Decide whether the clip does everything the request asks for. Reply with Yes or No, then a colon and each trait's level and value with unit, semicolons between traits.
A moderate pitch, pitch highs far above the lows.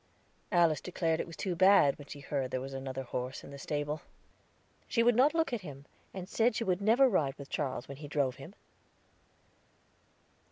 Yes: medium, 155 Hz; wide, 6.4 semitones